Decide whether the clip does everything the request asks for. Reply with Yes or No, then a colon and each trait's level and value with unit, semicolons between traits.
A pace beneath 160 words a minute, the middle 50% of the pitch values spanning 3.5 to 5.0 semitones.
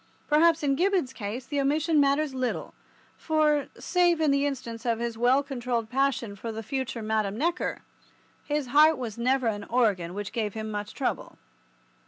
No: average, 170 wpm; average, 4.7 semitones